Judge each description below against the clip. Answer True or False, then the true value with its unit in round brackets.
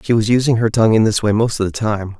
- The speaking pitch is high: False (110 Hz)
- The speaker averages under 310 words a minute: False (330 wpm)